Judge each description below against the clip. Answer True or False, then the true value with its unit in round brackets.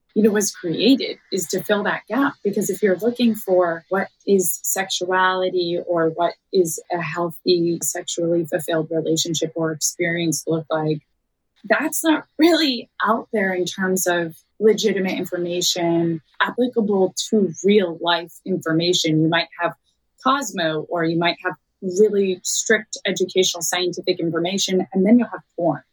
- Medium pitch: True (180 Hz)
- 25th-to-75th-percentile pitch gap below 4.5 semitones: True (3.6 semitones)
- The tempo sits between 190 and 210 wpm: False (145 wpm)